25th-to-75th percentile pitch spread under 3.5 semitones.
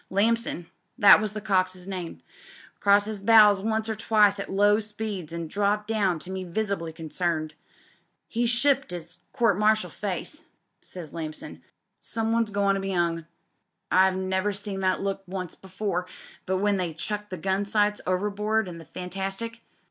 Yes: average, 2.7 semitones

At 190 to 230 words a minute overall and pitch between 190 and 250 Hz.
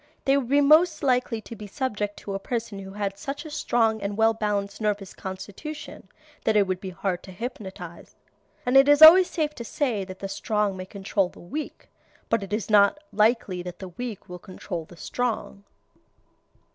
Yes: average, 195 wpm; high, 210 Hz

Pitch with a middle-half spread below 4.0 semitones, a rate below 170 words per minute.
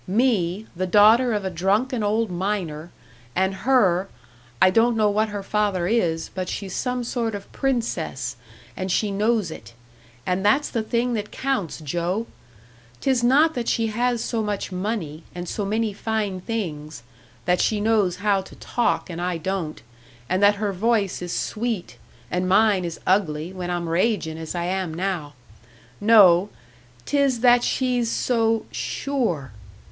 No: average, 4.3 semitones; average, 160 wpm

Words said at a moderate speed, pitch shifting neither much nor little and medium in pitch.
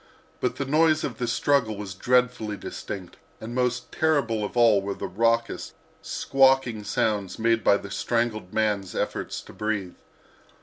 No: average, 155 wpm; average, 3.3 semitones; low, 115 Hz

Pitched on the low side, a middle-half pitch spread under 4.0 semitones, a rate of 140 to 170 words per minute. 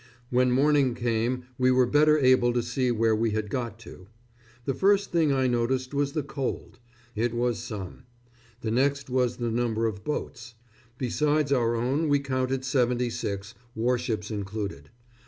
Yes: low, 125 Hz; average, 2.8 semitones; average, 160 wpm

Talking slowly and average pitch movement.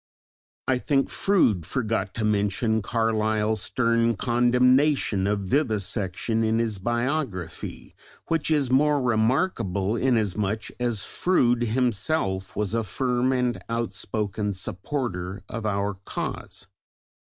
Yes: slow, 105 wpm; average, 3.7 semitones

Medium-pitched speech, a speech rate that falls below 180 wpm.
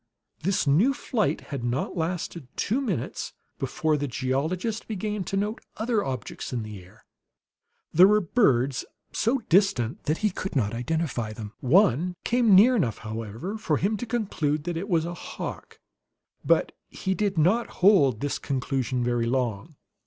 Yes: medium, 160 Hz; average, 160 wpm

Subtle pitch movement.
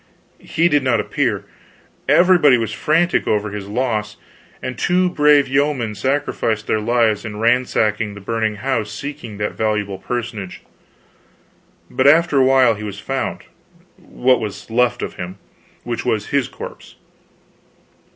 No: average, 4.3 semitones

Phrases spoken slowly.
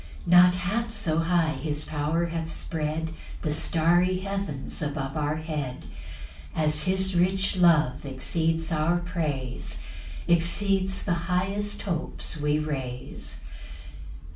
Yes: slow, 115 wpm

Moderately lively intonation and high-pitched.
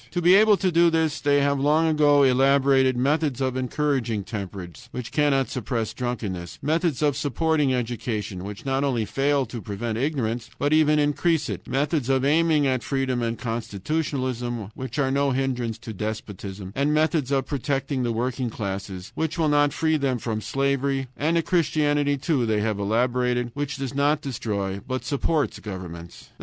No: average, 4.1 semitones; low, 135 Hz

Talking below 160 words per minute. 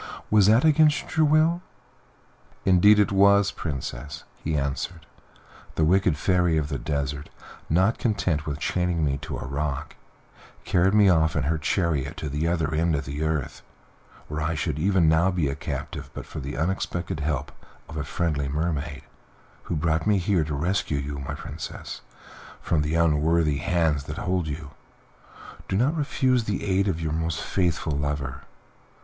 No: average, 165 wpm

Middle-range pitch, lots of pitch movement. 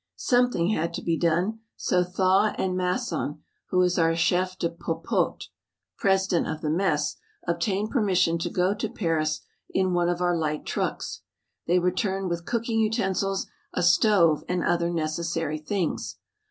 No: medium, 180 Hz; narrow, 2.4 semitones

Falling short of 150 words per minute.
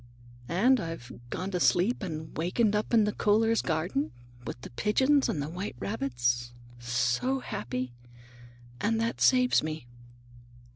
Yes: average, 140 wpm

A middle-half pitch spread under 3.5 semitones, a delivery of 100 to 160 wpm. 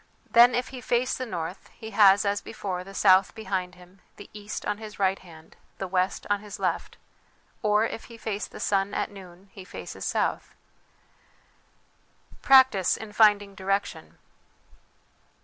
Yes: narrow, 2.5 semitones; average, 155 wpm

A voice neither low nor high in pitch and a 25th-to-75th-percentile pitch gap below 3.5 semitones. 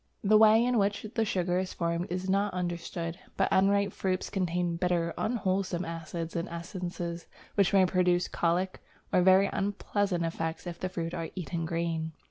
Yes: medium, 180 Hz; narrow, 2.5 semitones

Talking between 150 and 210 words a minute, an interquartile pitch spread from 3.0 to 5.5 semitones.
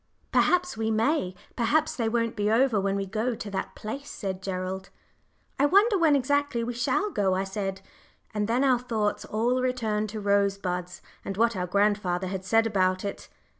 Yes: average, 180 wpm; average, 4.2 semitones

